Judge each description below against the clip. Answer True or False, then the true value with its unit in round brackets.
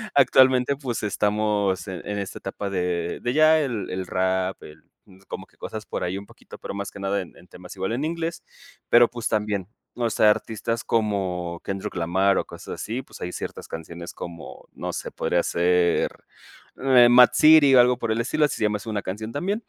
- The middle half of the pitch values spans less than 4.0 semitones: False (4.7 semitones)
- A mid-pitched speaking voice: False (105 Hz)